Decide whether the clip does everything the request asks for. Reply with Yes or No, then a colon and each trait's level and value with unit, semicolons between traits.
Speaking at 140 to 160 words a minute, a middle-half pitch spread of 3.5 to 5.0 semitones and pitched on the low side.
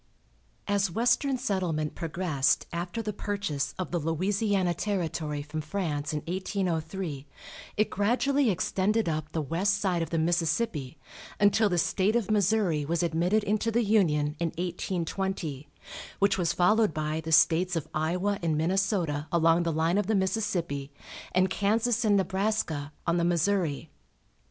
No: average, 145 wpm; average, 4.2 semitones; medium, 180 Hz